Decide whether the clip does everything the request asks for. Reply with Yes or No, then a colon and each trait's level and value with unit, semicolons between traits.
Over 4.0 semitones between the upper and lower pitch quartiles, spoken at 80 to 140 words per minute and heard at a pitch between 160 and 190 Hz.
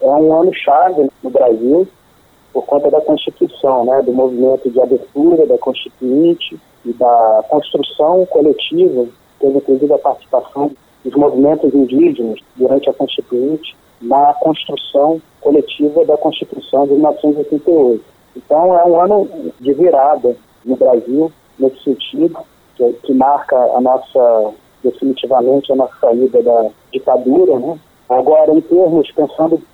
No: average, 4.9 semitones; average, 130 wpm; medium, 145 Hz